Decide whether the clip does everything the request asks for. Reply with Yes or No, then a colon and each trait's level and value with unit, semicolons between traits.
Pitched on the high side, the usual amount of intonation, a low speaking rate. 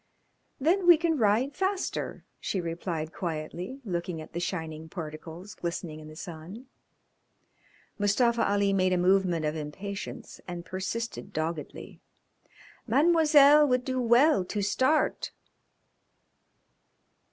No: high, 195 Hz; wide, 7.3 semitones; slow, 115 wpm